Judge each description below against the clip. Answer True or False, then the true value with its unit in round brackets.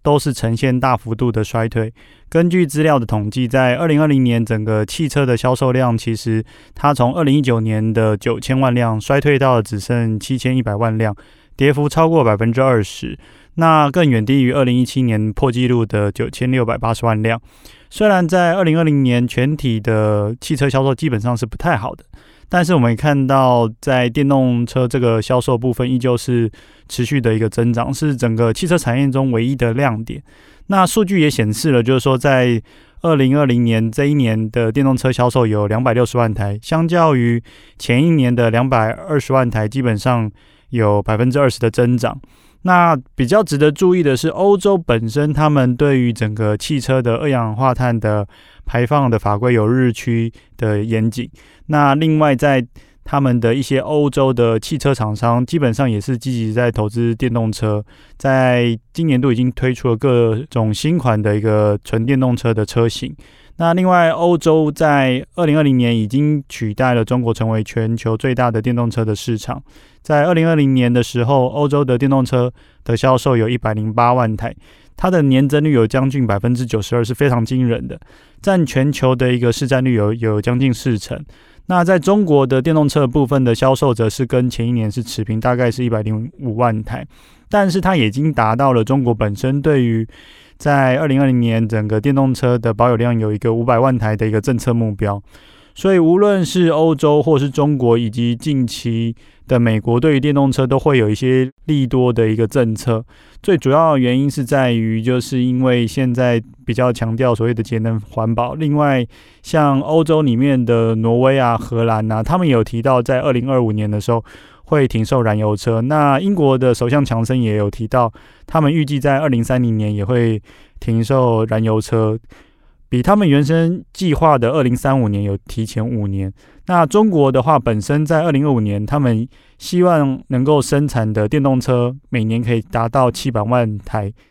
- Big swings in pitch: False (3.6 semitones)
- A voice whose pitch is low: True (125 Hz)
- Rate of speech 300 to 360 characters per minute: False (285 characters per minute)